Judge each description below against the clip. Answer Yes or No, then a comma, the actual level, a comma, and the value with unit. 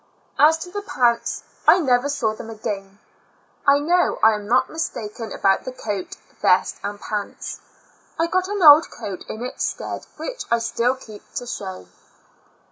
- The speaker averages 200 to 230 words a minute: No, average, 165 wpm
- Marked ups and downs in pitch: Yes, wide, 6.6 semitones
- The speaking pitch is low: No, high, 240 Hz